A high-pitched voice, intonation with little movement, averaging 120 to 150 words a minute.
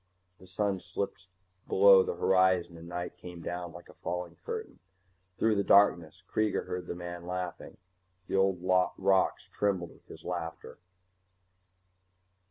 No: very low, 90 Hz; narrow, 1.7 semitones; average, 140 wpm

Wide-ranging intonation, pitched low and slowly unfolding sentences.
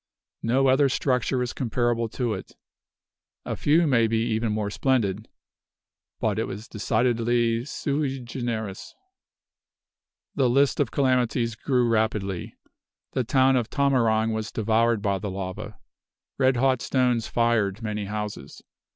No: average, 3.0 semitones; low, 115 Hz; slow, 130 wpm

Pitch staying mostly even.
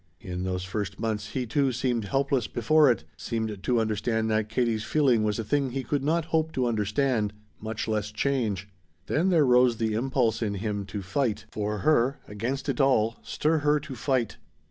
No: average, 4.2 semitones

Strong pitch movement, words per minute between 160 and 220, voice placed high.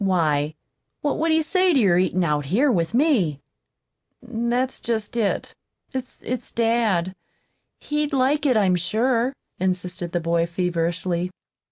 No: wide, 6.8 semitones; slow, 135 wpm; high, 210 Hz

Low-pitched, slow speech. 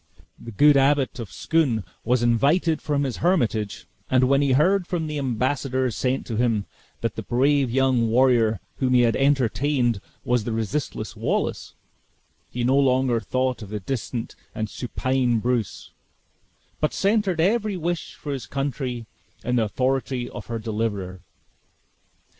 No: low, 130 Hz; average, 150 wpm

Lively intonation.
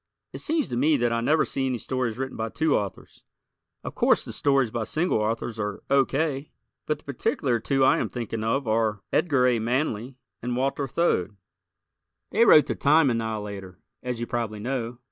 No: average, 3.7 semitones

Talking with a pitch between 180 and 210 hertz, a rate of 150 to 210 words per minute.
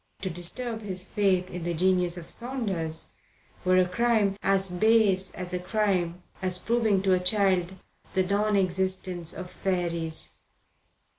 No: medium, 185 Hz; average, 140 wpm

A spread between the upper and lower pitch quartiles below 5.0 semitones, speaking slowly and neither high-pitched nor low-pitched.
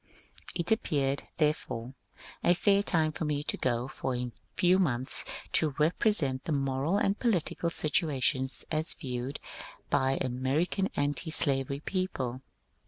Yes: average, 4.5 semitones; slow, 130 wpm; medium, 145 Hz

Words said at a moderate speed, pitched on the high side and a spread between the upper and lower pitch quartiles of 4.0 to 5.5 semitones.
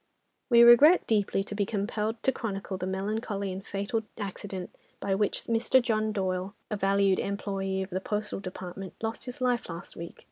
No: average, 175 wpm; high, 200 Hz; narrow, 2.6 semitones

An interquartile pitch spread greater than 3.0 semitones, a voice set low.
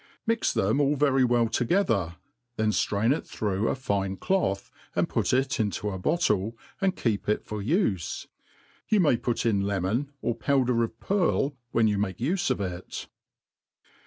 Yes: wide, 5.6 semitones; low, 115 Hz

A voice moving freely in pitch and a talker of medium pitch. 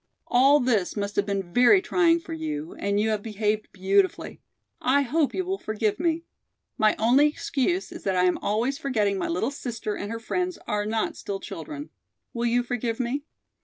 No: wide, 6.1 semitones; high, 235 Hz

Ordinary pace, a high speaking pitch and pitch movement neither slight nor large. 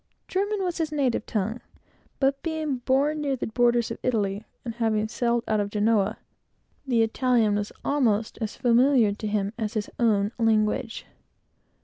Yes: average, 155 wpm; high, 230 Hz; average, 3.8 semitones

